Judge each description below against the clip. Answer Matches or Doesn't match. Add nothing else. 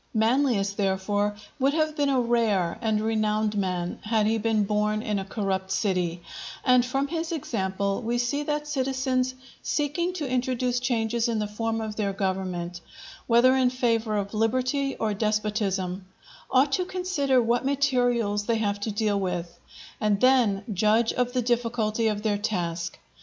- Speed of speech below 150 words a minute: Doesn't match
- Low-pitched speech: Doesn't match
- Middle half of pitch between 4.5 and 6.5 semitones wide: Doesn't match